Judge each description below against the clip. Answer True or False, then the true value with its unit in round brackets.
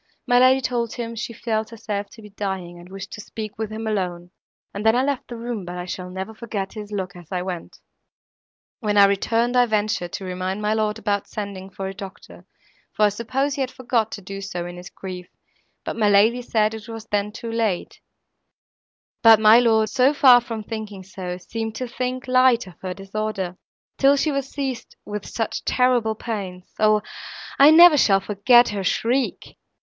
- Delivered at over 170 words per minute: True (195 wpm)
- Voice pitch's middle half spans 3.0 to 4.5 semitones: True (3.5 semitones)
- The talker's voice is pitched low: False (215 Hz)